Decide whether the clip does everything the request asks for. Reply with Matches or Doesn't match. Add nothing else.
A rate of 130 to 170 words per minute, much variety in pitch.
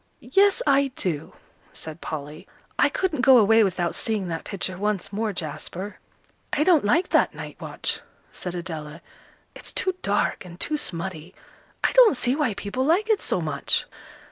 Matches